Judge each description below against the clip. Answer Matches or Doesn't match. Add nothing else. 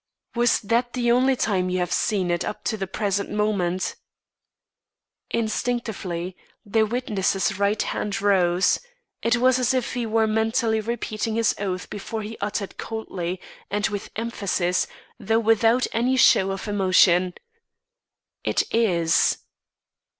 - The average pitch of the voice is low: Doesn't match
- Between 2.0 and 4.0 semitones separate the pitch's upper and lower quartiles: Matches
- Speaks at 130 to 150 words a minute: Matches